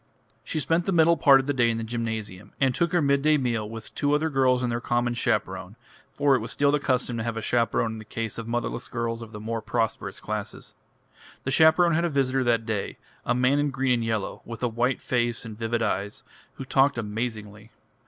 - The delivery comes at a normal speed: No, fast, 225 wpm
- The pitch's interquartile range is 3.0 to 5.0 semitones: Yes, average, 3.4 semitones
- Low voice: Yes, low, 120 Hz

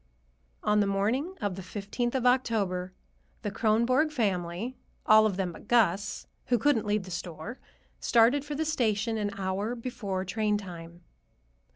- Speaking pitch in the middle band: No, high, 210 Hz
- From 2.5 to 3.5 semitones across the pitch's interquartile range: No, average, 4.1 semitones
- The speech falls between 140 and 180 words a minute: Yes, average, 155 wpm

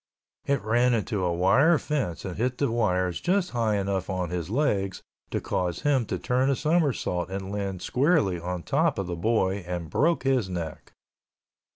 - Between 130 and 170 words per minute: No, average, 180 wpm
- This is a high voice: No, low, 100 Hz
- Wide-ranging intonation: Yes, wide, 6.2 semitones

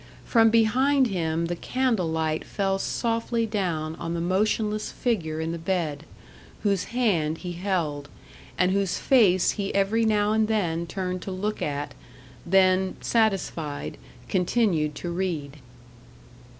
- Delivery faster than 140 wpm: No, slow, 135 wpm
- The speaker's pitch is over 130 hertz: Yes, high, 190 Hz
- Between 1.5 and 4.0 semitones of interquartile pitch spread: No, average, 4.7 semitones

